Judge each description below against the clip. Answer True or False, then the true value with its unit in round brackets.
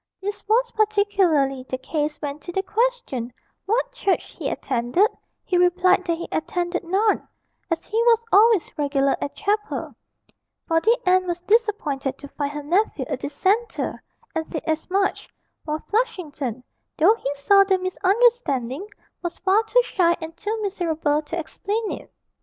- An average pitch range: False (5.8 semitones)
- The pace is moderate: True (155 wpm)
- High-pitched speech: True (360 Hz)